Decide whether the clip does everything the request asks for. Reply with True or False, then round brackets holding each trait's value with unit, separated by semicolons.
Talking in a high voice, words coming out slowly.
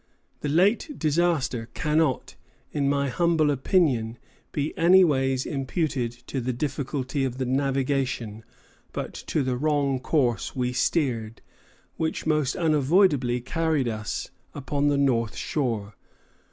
False (140 Hz; 120 wpm)